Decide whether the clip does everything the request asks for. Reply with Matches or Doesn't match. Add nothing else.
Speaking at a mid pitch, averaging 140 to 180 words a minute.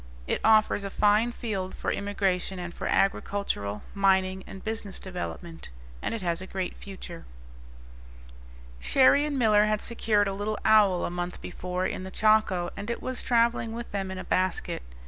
Doesn't match